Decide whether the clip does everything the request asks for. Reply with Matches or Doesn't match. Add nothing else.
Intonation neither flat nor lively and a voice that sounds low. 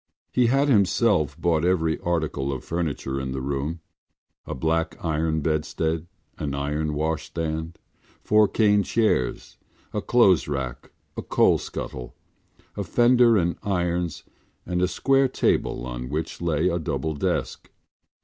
Matches